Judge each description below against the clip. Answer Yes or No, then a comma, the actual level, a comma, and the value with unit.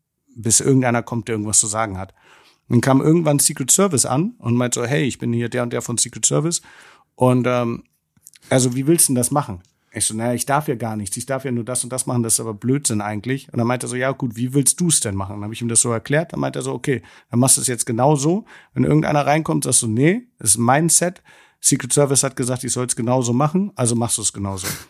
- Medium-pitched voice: No, low, 125 Hz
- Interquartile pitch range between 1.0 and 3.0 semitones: No, average, 3.4 semitones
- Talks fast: Yes, fast, 275 wpm